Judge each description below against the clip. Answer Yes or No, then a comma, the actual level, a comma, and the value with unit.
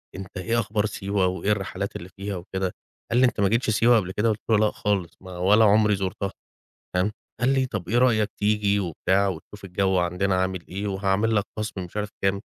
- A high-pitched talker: No, low, 100 Hz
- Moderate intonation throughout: No, narrow, 2.2 semitones